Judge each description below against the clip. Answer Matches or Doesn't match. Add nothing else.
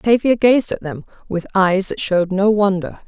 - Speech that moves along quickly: Doesn't match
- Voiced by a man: Doesn't match